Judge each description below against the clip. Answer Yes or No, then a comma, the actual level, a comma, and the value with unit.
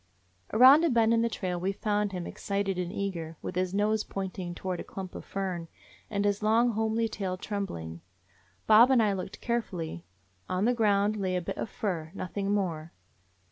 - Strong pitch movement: No, average, 3.0 semitones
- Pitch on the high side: Yes, high, 200 Hz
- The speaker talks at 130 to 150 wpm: No, average, 190 wpm